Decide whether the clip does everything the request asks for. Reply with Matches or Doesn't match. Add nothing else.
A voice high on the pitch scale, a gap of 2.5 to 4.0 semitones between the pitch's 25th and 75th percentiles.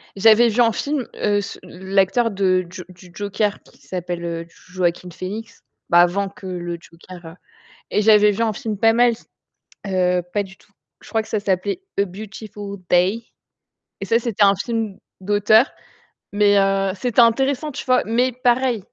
Matches